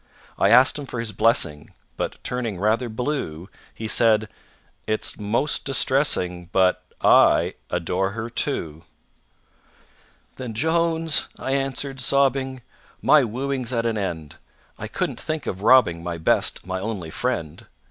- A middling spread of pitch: No, wide, 6.1 semitones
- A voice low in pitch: Yes, low, 115 Hz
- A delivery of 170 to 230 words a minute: No, slow, 135 wpm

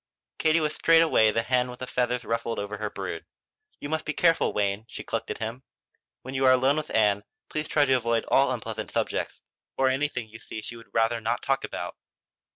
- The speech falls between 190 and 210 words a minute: Yes, fast, 205 wpm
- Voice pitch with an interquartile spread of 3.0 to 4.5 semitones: Yes, average, 3.5 semitones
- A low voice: Yes, low, 125 Hz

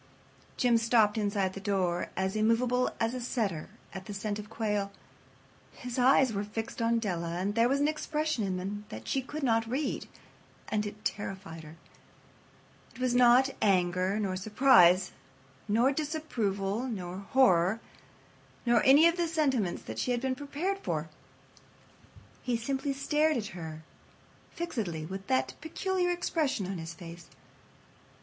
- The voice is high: Yes, high, 225 Hz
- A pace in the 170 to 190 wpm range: No, average, 150 wpm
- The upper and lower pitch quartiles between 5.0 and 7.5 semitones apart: Yes, wide, 5.6 semitones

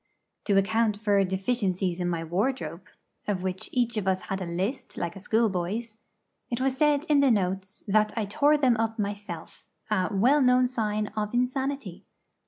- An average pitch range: Yes, average, 4.6 semitones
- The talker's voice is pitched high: Yes, high, 210 Hz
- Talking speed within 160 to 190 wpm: Yes, average, 175 wpm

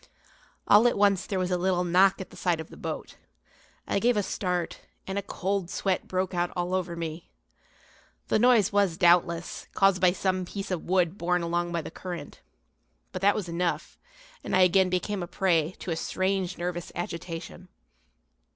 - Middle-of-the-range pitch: Yes, medium, 180 Hz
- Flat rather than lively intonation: Yes, narrow, 1.9 semitones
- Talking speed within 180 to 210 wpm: Yes, average, 185 wpm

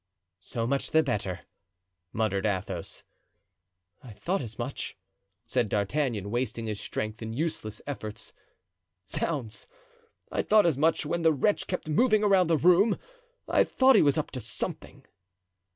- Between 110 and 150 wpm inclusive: Yes, average, 145 wpm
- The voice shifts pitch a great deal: Yes, wide, 7.4 semitones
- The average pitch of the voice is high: No, low, 130 Hz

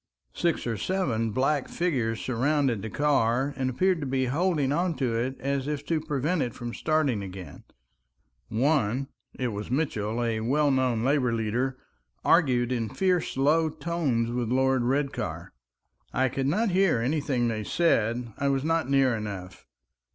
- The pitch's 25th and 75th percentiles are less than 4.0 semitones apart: No, average, 4.3 semitones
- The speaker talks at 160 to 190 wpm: No, average, 150 wpm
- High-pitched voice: No, low, 130 Hz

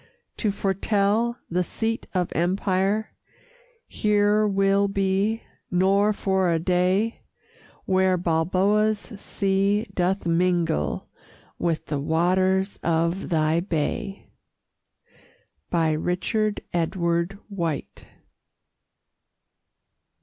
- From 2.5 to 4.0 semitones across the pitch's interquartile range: Yes, average, 2.9 semitones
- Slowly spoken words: Yes, slow, 80 wpm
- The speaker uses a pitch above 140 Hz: Yes, high, 190 Hz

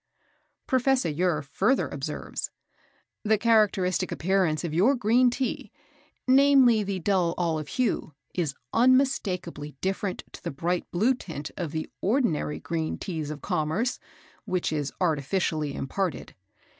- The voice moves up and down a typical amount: No, wide, 6.5 semitones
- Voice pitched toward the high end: No, medium, 180 Hz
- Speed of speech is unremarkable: No, slow, 125 wpm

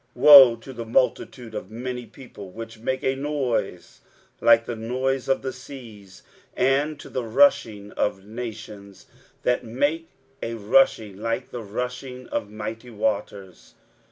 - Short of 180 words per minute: Yes, average, 145 wpm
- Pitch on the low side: Yes, low, 115 Hz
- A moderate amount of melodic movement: Yes, average, 3.4 semitones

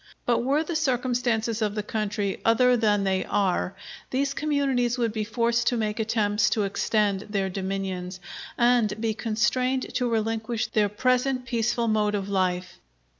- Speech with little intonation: No, average, 3.1 semitones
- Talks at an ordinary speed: Yes, average, 155 wpm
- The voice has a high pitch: Yes, high, 220 Hz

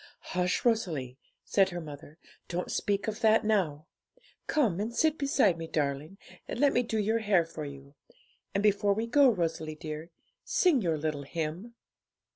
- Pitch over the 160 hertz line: Yes, medium, 185 Hz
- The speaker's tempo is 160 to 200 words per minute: Yes, average, 165 wpm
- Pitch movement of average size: No, wide, 6.1 semitones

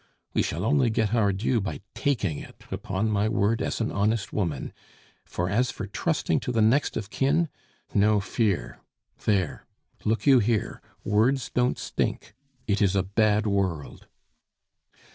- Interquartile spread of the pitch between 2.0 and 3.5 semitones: Yes, average, 3.0 semitones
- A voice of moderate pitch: No, low, 105 Hz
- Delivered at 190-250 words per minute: No, average, 155 wpm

